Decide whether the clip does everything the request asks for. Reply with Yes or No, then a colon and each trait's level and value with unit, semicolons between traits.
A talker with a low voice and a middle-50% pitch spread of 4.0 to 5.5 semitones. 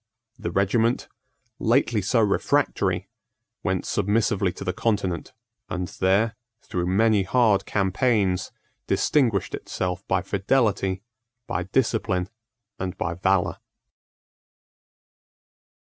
No: low, 100 Hz; average, 3.3 semitones